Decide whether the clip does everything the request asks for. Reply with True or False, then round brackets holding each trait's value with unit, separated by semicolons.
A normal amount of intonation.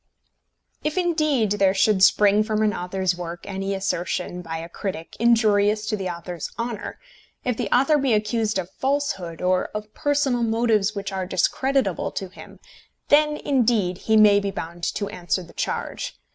True (4.3 semitones)